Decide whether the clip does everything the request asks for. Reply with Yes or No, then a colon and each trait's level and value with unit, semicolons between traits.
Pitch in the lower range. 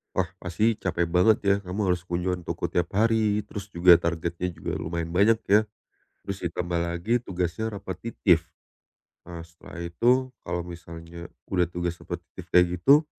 Yes: very low, 90 Hz